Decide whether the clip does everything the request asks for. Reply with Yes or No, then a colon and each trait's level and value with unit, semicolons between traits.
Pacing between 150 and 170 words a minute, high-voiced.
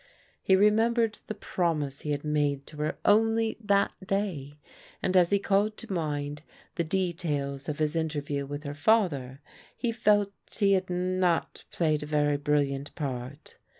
No: average, 155 wpm; medium, 160 Hz